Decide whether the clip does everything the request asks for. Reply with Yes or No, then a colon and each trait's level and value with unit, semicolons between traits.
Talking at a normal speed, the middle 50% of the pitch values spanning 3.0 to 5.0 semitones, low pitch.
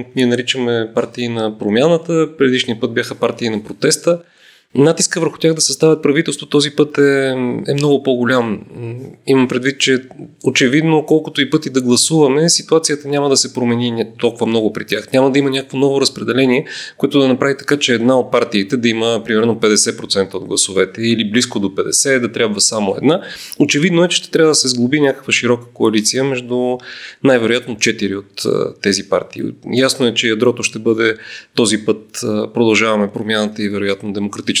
Yes: average, 170 wpm; average, 3.7 semitones; low, 125 Hz